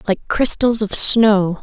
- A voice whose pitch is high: Yes, high, 210 Hz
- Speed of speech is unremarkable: Yes, average, 150 wpm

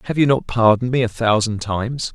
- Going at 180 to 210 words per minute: No, fast, 225 wpm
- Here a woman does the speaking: No, male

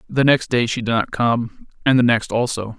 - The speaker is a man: Yes, male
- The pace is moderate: No, fast, 235 wpm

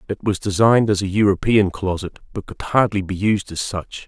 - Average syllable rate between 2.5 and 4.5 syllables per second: No, 5.3 syllables/s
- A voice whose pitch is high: No, low, 100 Hz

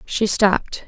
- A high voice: Yes, high, 200 Hz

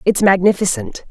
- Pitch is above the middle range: Yes, high, 200 Hz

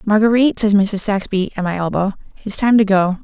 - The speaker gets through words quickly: Yes, fast, 220 wpm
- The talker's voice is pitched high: Yes, high, 205 Hz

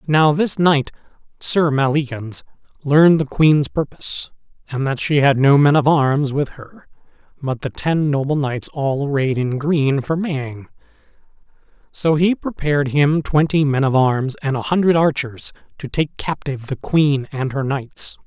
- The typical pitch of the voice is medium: Yes, medium, 145 Hz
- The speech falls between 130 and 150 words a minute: No, average, 165 wpm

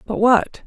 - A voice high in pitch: Yes, high, 230 Hz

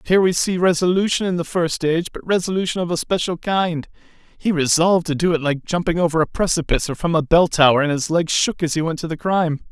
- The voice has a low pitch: No, medium, 170 Hz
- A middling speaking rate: No, fast, 240 wpm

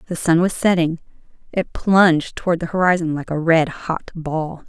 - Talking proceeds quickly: No, average, 180 wpm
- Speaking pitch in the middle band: Yes, medium, 170 Hz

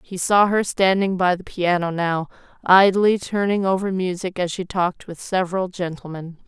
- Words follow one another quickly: No, average, 165 wpm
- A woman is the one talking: Yes, female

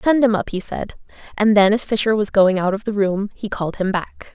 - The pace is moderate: No, fast, 265 wpm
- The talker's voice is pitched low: No, high, 205 Hz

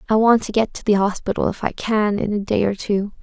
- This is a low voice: No, high, 210 Hz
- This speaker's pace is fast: Yes, fast, 280 wpm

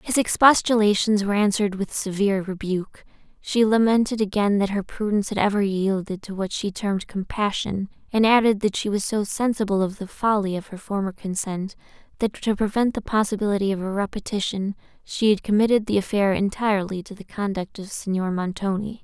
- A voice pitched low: No, high, 205 Hz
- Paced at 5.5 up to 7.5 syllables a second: Yes, 5.7 syllables/s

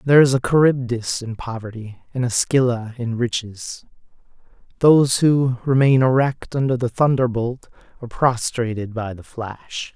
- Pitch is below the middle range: Yes, low, 125 Hz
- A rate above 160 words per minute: No, average, 140 wpm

